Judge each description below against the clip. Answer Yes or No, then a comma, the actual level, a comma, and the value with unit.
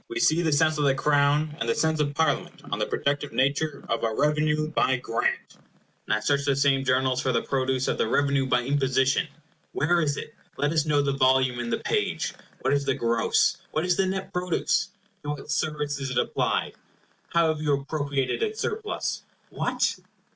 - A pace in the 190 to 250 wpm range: Yes, average, 200 wpm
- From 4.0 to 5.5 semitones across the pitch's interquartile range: No, average, 2.8 semitones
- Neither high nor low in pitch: Yes, medium, 145 Hz